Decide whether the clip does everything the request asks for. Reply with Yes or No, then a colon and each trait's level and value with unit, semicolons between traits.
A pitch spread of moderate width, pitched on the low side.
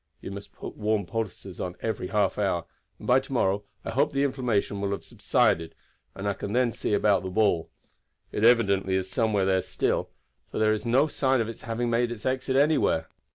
Yes: average, 3.9 semitones; low, 110 Hz